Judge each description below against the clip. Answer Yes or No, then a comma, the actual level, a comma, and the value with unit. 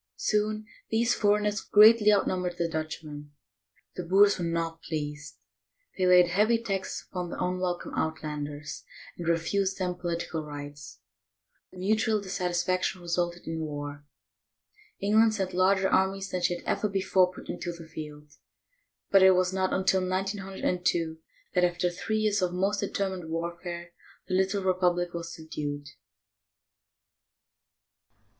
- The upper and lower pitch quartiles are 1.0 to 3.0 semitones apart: Yes, average, 2.7 semitones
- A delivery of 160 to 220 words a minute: No, slow, 135 wpm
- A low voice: No, medium, 180 Hz